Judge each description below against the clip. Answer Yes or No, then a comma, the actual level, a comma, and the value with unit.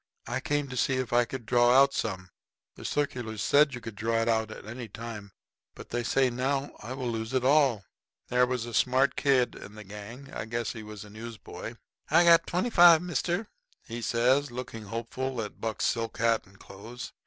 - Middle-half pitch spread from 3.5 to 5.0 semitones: No, average, 3.0 semitones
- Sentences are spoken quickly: Yes, fast, 210 wpm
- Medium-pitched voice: No, low, 120 Hz